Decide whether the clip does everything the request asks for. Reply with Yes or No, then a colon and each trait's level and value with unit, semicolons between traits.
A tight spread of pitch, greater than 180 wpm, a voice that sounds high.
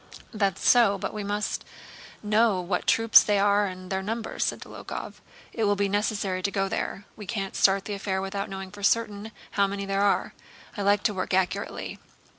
Yes: narrow, 1.3 semitones; average, 195 wpm; high, 200 Hz